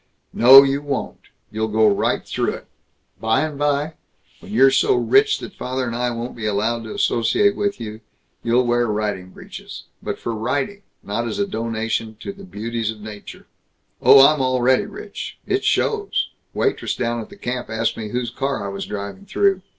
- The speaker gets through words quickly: No, average, 185 wpm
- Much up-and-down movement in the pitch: No, average, 4.5 semitones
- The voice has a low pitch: Yes, low, 120 Hz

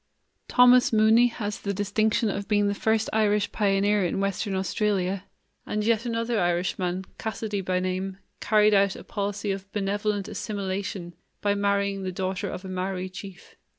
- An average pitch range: No, narrow, 1.8 semitones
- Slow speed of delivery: No, average, 155 wpm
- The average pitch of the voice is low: No, high, 200 Hz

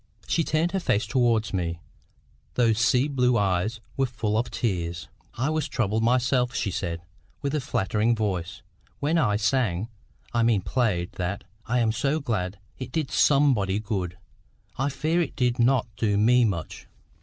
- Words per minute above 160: No, average, 155 wpm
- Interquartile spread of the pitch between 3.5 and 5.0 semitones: Yes, average, 4.7 semitones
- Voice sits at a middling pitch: No, low, 115 Hz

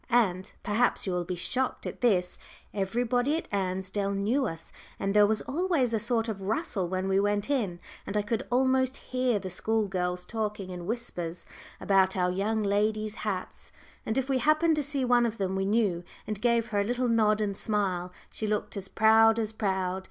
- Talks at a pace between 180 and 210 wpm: Yes, average, 200 wpm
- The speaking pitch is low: No, high, 210 Hz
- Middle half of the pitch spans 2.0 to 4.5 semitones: Yes, average, 3.8 semitones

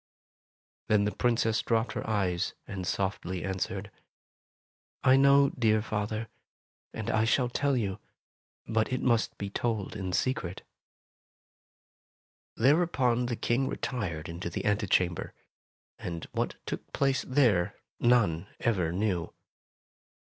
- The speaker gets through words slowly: Yes, slow, 125 wpm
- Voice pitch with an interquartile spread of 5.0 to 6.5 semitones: No, average, 4.5 semitones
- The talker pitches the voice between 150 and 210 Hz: No, low, 110 Hz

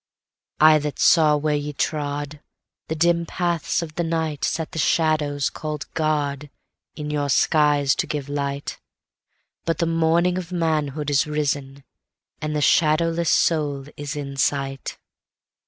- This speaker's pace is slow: Yes, slow, 125 wpm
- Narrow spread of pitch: Yes, narrow, 2.0 semitones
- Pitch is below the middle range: No, medium, 150 Hz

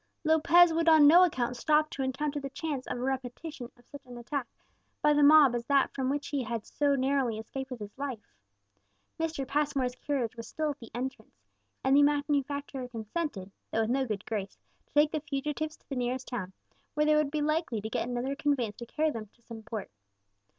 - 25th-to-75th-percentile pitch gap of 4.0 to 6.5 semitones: No, average, 3.6 semitones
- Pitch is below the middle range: No, very high, 270 Hz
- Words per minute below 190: No, fast, 205 wpm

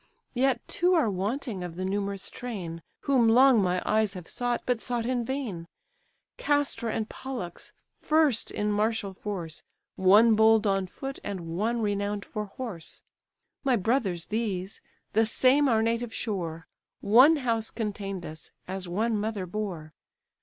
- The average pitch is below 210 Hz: No, high, 215 Hz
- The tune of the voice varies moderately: Yes, average, 4.2 semitones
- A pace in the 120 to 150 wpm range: Yes, average, 145 wpm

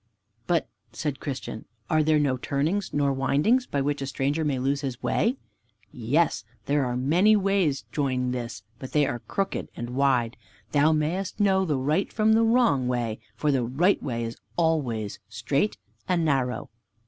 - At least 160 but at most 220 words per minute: Yes, average, 170 wpm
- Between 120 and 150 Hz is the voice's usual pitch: Yes, medium, 140 Hz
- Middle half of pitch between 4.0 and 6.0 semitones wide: Yes, average, 5.0 semitones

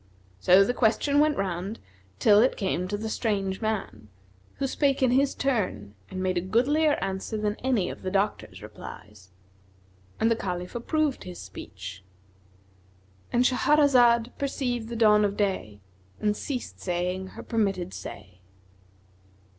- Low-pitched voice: No, high, 205 Hz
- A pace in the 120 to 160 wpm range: Yes, average, 140 wpm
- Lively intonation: Yes, wide, 5.7 semitones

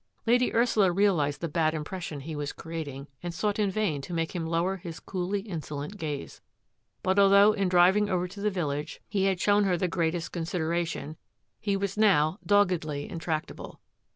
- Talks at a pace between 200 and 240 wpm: No, average, 175 wpm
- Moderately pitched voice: Yes, medium, 175 Hz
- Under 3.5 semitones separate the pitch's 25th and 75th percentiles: No, average, 3.8 semitones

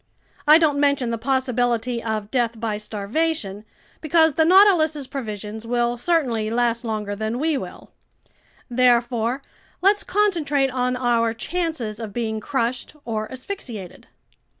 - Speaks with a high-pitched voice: Yes, high, 245 Hz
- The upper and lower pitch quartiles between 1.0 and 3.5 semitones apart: No, average, 4.8 semitones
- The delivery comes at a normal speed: No, slow, 125 wpm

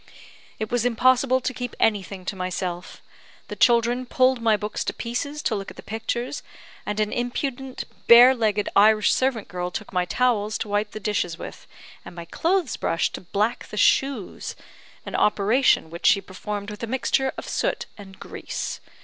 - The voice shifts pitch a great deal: No, average, 3.8 semitones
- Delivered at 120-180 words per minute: Yes, average, 175 wpm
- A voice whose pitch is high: Yes, high, 220 Hz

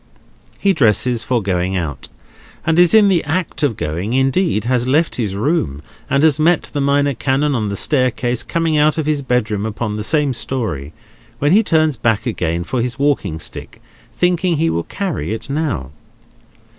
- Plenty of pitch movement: Yes, wide, 6.6 semitones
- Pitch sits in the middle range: No, low, 130 Hz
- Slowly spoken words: No, average, 170 wpm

